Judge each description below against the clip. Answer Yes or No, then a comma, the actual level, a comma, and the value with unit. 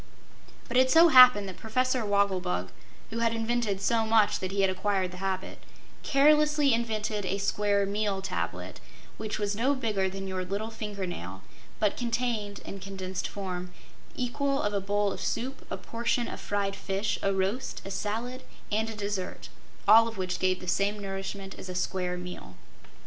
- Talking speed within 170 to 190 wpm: Yes, average, 175 wpm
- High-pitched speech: Yes, high, 205 Hz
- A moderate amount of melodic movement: Yes, average, 3.1 semitones